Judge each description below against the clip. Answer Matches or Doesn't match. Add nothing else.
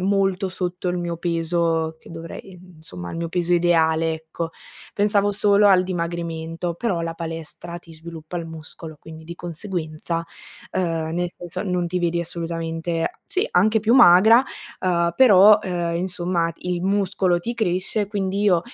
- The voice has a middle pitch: Matches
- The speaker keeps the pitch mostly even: Matches